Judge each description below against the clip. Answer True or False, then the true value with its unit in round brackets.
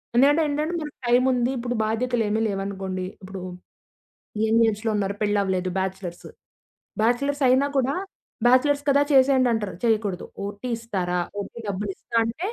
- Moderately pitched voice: False (225 Hz)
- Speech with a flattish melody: False (4.4 semitones)